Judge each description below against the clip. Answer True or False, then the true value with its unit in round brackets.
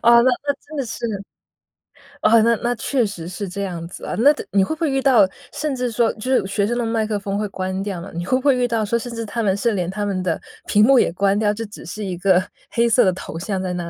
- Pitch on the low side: False (210 Hz)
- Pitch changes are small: False (3.9 semitones)